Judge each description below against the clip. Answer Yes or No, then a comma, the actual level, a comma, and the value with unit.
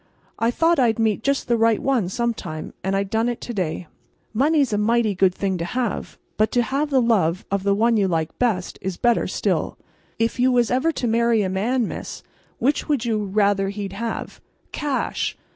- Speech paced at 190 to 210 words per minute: Yes, fast, 205 wpm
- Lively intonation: No, average, 3.8 semitones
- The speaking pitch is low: No, high, 225 Hz